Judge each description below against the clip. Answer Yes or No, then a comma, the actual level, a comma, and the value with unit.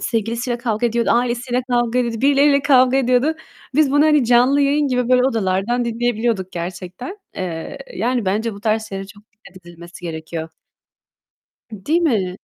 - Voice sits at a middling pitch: No, high, 235 Hz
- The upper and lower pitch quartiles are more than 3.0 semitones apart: Yes, average, 4.6 semitones